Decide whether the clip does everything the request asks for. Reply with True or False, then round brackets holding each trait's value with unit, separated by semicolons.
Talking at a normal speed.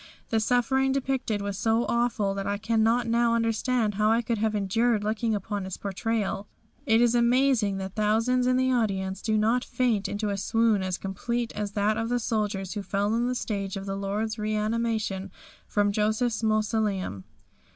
True (180 wpm)